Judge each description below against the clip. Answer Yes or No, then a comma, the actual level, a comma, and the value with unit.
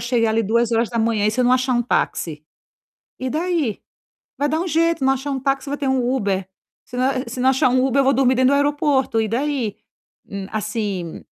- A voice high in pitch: Yes, very high, 255 Hz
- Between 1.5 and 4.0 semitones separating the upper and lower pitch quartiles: Yes, average, 3.5 semitones